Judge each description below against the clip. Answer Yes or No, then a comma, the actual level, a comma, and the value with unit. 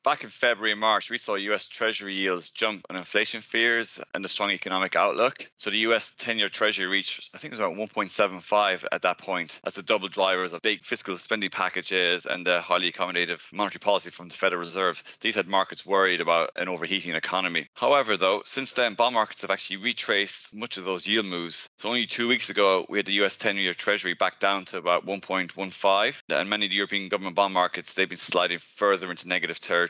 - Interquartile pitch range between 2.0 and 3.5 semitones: Yes, average, 2.9 semitones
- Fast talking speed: Yes, fast, 215 wpm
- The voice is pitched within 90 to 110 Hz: Yes, very low, 95 Hz